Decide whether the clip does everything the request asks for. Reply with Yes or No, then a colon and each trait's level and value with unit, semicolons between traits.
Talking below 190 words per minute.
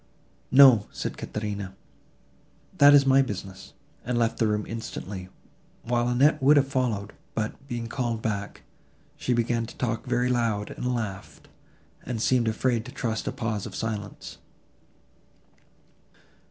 Yes: average, 140 wpm